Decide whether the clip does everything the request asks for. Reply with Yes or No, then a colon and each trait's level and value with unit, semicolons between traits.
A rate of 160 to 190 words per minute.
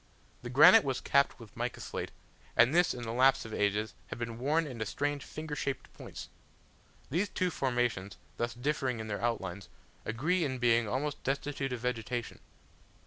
Yes: average, 170 wpm